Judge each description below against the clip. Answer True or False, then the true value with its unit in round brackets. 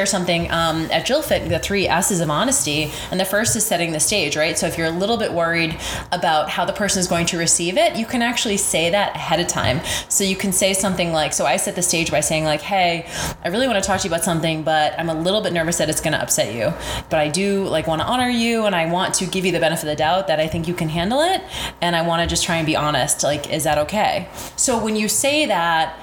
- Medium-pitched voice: True (170 Hz)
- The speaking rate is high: True (280 wpm)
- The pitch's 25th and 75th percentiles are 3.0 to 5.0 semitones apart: True (3.6 semitones)